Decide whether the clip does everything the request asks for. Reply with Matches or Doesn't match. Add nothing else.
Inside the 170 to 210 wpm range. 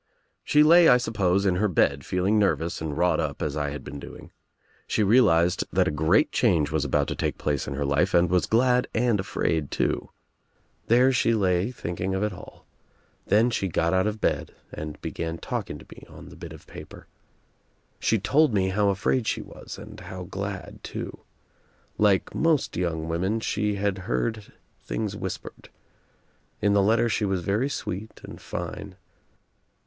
Matches